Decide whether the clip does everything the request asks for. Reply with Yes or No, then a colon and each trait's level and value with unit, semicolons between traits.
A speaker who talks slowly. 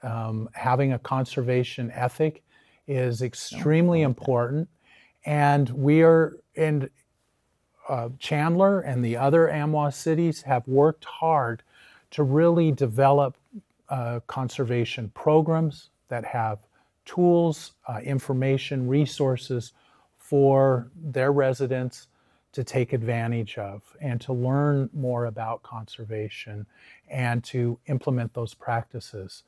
Yes: slow, 105 wpm